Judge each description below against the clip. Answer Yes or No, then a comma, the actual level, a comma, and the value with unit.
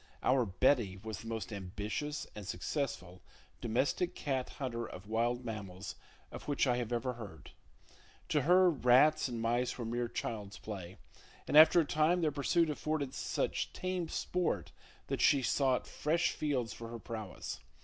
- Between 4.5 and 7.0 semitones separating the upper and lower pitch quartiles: Yes, average, 5.1 semitones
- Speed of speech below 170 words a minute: Yes, average, 160 wpm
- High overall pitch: No, low, 120 Hz